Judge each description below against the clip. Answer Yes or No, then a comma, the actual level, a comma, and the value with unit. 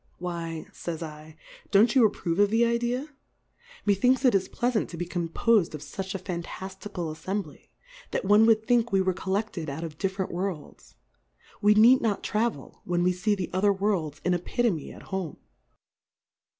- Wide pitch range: No, average, 4.0 semitones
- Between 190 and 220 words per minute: No, average, 170 wpm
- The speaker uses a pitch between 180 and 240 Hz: Yes, high, 190 Hz